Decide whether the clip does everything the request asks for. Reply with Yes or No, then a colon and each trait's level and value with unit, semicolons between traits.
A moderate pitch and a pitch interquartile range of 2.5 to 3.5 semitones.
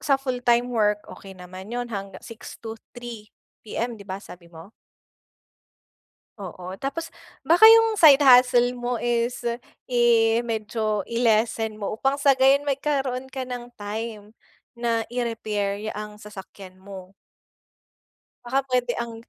No: high, 235 Hz; average, 3.1 semitones